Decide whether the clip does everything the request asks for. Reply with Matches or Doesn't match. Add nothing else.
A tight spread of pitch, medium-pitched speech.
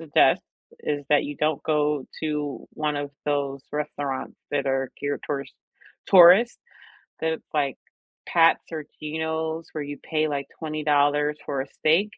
Matches